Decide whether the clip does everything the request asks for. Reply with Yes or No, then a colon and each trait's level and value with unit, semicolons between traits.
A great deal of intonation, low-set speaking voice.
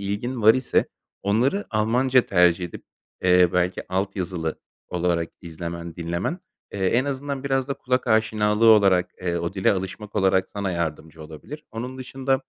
Yes: wide, 6.0 semitones; low, 100 Hz